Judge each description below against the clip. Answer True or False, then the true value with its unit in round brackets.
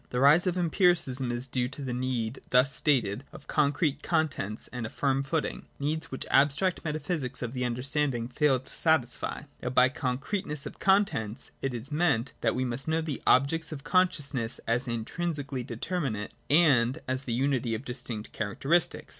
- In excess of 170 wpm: True (180 wpm)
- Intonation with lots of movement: False (4.0 semitones)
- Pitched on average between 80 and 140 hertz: True (135 Hz)